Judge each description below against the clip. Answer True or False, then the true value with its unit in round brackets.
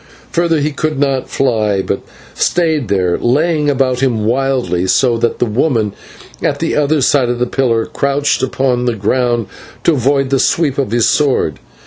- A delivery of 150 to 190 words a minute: True (170 wpm)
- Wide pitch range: False (3.5 semitones)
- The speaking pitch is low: True (130 Hz)